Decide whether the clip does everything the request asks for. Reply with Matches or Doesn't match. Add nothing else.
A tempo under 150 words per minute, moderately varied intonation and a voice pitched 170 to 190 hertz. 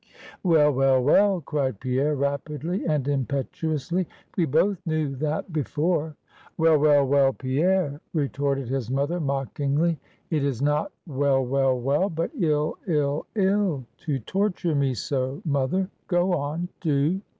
Doesn't match